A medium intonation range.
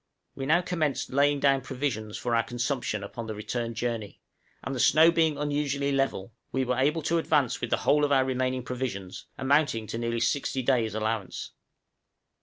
Yes: average, 3.7 semitones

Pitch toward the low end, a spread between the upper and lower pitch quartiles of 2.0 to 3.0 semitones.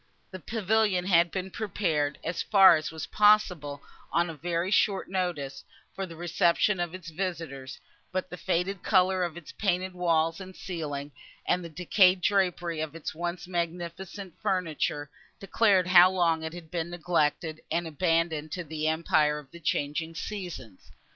No: medium, 175 Hz; average, 2.7 semitones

